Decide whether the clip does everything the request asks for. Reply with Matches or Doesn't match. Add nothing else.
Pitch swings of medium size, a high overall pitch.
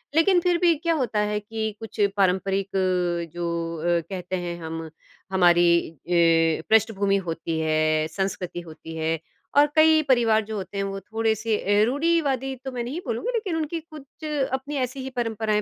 Doesn't match